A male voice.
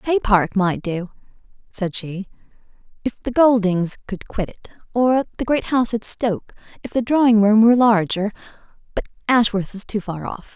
No: female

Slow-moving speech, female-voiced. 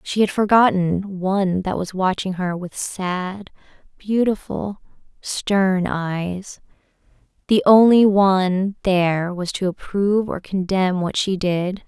Yes: slow, 120 wpm; female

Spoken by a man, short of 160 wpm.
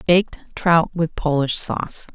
No: female; average, 140 wpm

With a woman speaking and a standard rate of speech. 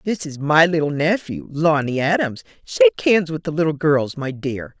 Yes: female; average, 175 wpm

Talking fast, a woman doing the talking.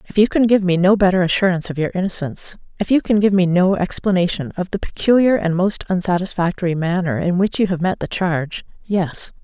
No: average, 195 wpm; female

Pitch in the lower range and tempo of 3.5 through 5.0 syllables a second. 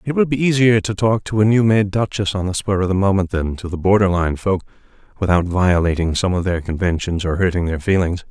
No: very low, 95 Hz; 5.9 syllables/s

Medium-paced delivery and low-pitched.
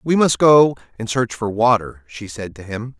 No: fast, 220 wpm; low, 115 Hz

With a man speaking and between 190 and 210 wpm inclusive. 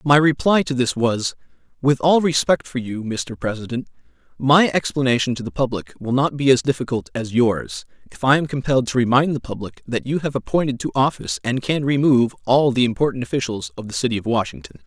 Yes: male; average, 200 wpm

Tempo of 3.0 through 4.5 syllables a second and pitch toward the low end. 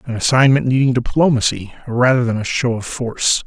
No: 5.6 syllables/s; low, 125 Hz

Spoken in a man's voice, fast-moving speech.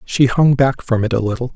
Yes: male; fast, 270 wpm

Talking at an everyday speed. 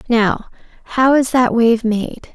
Yes: average, 155 wpm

